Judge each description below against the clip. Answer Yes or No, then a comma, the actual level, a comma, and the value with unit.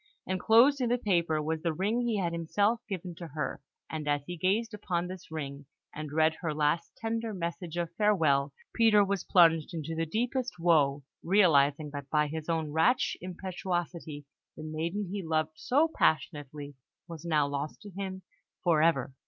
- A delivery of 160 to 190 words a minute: Yes, average, 170 wpm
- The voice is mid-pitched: Yes, medium, 170 Hz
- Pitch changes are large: No, average, 4.1 semitones